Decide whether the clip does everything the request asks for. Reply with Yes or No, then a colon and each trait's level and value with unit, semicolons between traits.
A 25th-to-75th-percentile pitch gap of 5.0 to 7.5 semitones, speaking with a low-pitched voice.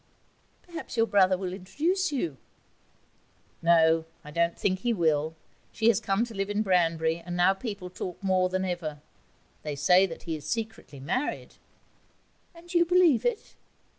No: wide, 5.4 semitones; medium, 185 Hz